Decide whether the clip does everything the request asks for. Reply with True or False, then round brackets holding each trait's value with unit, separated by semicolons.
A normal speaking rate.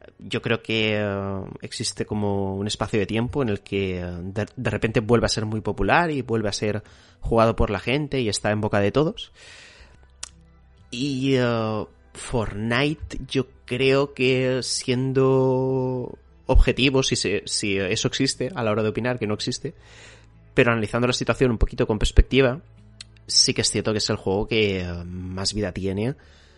True (175 wpm)